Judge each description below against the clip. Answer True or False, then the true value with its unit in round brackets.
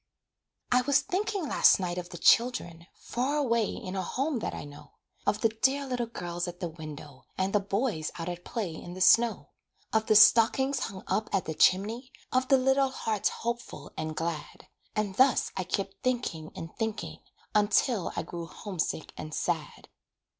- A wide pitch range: True (6.1 semitones)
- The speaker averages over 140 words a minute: True (180 wpm)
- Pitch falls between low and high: False (210 Hz)